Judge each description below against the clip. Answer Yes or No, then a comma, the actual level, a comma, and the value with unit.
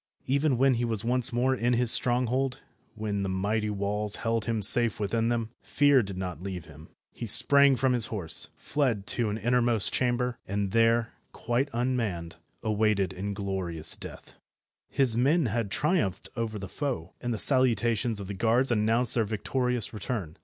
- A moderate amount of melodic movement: Yes, average, 3.5 semitones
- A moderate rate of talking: Yes, average, 165 wpm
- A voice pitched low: Yes, low, 115 Hz